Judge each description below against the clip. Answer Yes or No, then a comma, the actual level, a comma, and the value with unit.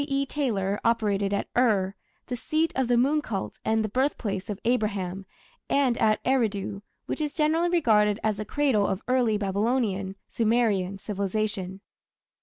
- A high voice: Yes, high, 215 Hz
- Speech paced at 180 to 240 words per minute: No, average, 150 wpm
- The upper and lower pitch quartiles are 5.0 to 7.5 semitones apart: No, average, 4.2 semitones